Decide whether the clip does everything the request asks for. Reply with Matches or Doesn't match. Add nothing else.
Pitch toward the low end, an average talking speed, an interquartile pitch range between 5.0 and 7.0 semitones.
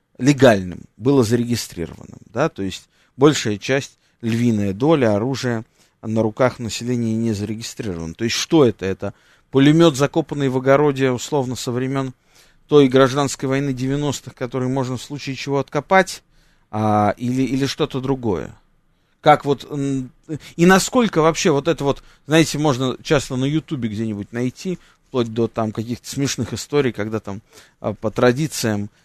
Doesn't match